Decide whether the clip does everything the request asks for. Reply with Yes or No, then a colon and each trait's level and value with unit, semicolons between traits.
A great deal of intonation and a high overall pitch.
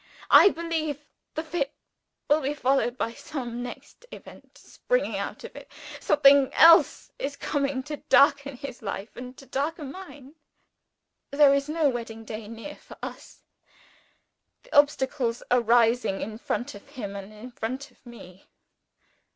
No: average, 3.7 semitones; very high, 270 Hz